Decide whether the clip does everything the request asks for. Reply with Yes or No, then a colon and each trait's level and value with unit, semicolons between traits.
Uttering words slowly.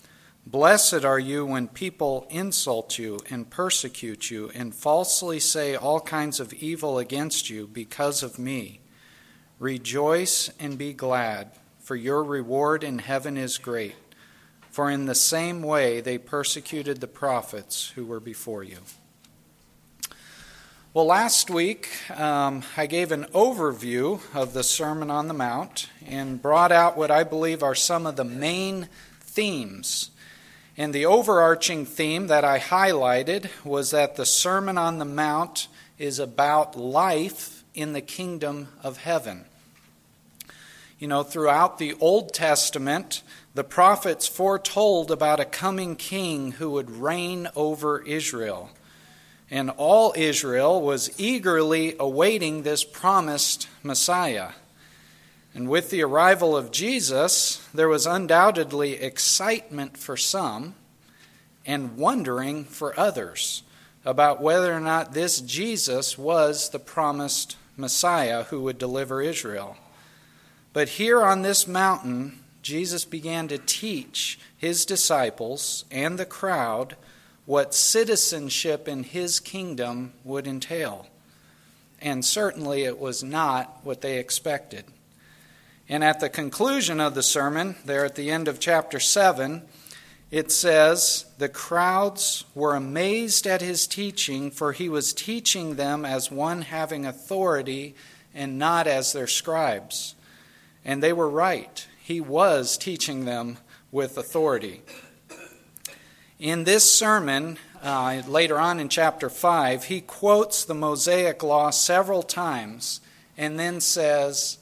Yes: slow, 130 wpm